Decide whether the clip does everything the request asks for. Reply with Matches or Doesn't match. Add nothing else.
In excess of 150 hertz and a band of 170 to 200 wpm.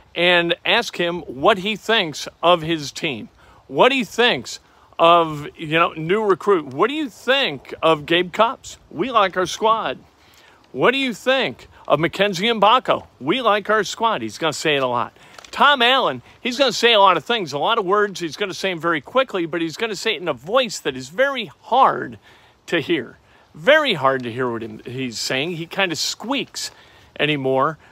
Matches